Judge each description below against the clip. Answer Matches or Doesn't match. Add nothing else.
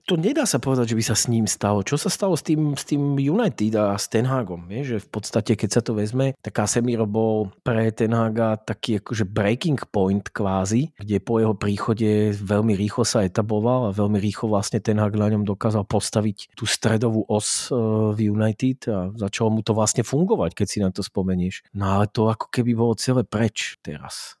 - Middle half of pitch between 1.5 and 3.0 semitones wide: Matches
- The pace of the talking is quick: Matches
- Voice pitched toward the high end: Doesn't match